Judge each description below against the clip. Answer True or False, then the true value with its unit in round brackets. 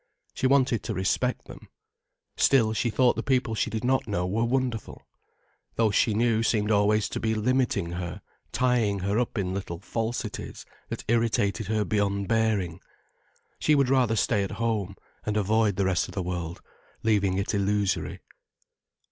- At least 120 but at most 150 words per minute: False (165 wpm)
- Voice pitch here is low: True (110 Hz)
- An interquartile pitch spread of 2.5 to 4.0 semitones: True (2.9 semitones)